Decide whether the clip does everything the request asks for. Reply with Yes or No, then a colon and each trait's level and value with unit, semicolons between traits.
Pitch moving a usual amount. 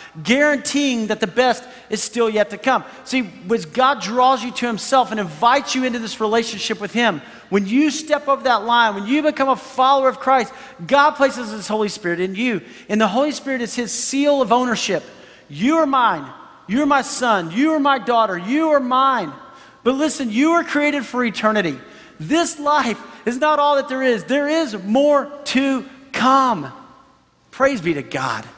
Yes: average, 3.8 semitones